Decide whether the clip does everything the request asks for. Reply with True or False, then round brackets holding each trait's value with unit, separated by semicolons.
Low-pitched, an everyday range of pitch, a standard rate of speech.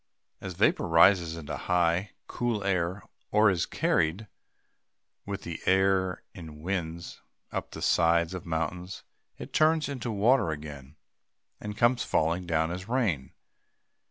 False (90 Hz; 3.6 semitones; 130 wpm)